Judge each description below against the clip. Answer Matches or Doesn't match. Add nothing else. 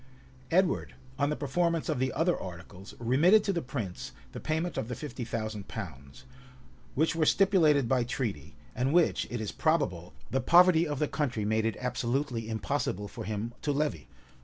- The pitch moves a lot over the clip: Matches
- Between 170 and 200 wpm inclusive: Matches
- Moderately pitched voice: Doesn't match